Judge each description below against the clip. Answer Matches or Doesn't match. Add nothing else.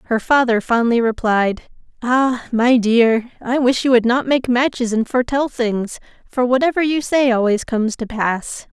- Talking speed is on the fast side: Doesn't match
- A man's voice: Doesn't match